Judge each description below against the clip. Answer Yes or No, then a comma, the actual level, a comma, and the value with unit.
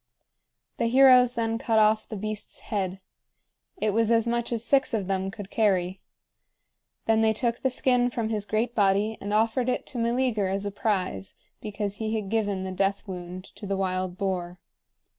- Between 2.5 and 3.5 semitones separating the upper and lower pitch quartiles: Yes, average, 3.0 semitones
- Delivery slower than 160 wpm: No, average, 180 wpm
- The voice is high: Yes, high, 215 Hz